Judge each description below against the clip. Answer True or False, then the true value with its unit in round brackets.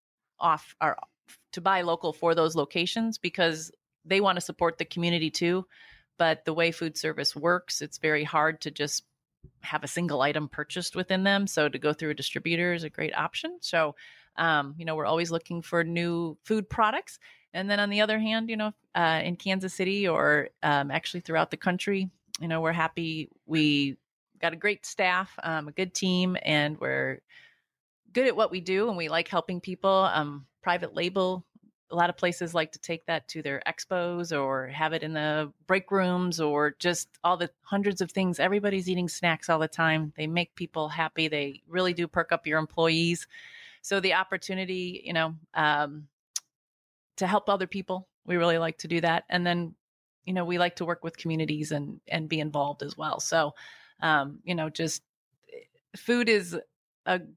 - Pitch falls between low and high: True (170 Hz)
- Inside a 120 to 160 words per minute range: False (190 wpm)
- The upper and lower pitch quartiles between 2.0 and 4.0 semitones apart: True (2.9 semitones)